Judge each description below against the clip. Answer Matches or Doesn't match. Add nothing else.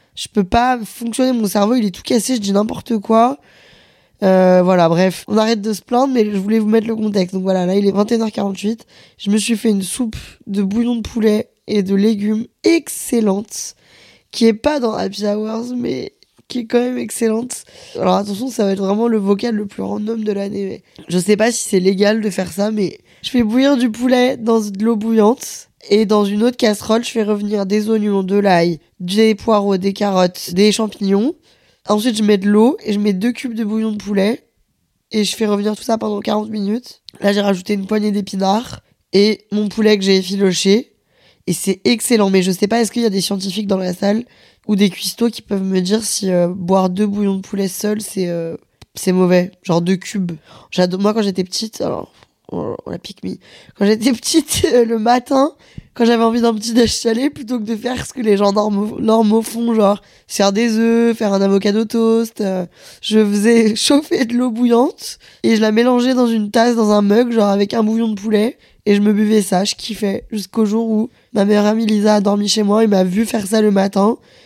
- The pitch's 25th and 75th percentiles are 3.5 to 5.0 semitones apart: Doesn't match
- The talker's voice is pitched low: Doesn't match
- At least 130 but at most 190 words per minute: Doesn't match